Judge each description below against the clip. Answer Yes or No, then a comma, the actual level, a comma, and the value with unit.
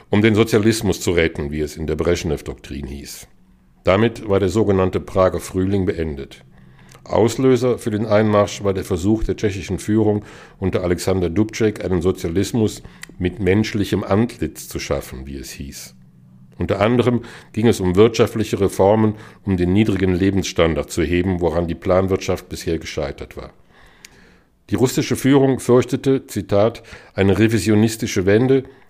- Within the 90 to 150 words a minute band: Yes, average, 140 wpm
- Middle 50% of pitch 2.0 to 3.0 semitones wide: No, average, 3.8 semitones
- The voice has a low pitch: Yes, low, 100 Hz